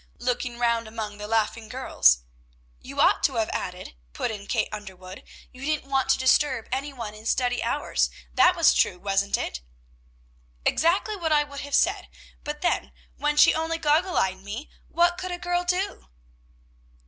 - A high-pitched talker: Yes, very high, 260 Hz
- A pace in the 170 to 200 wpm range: Yes, average, 175 wpm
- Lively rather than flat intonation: Yes, wide, 6.8 semitones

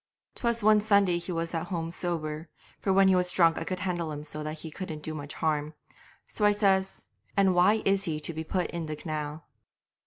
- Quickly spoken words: Yes, fast, 225 wpm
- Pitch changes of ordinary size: Yes, average, 3.7 semitones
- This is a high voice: No, medium, 170 Hz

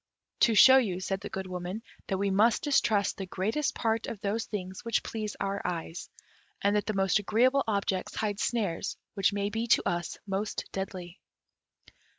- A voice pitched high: Yes, high, 200 Hz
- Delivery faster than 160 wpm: Yes, average, 175 wpm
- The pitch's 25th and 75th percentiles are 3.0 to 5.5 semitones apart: No, narrow, 2.6 semitones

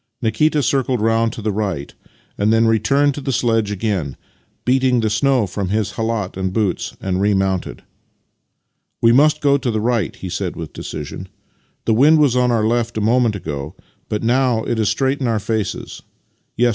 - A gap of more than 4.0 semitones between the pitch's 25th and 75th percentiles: No, average, 3.6 semitones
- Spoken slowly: No, average, 185 wpm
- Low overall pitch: Yes, low, 115 Hz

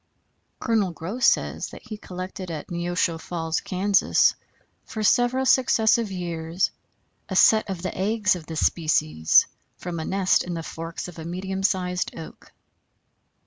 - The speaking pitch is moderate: Yes, medium, 180 Hz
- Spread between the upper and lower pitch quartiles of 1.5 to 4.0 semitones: Yes, average, 3.6 semitones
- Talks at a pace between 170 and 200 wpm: No, average, 145 wpm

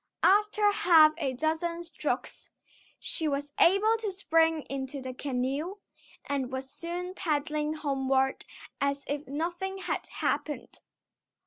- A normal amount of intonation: Yes, average, 4.3 semitones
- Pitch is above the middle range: Yes, very high, 310 Hz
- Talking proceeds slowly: Yes, slow, 120 wpm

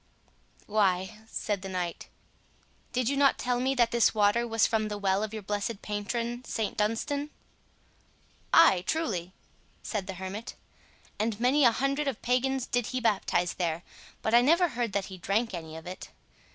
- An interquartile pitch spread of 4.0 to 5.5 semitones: Yes, average, 4.3 semitones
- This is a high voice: Yes, high, 220 Hz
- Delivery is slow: No, average, 170 wpm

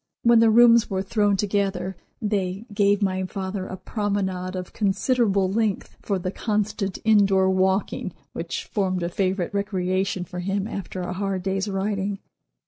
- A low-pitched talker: No, high, 195 Hz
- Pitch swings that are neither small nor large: No, narrow, 1.7 semitones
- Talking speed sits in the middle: Yes, average, 150 wpm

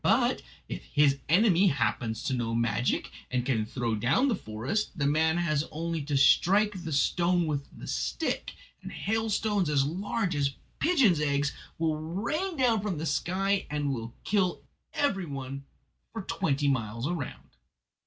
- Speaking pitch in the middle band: Yes, medium, 155 Hz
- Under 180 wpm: Yes, average, 155 wpm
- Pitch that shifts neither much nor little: No, wide, 6.2 semitones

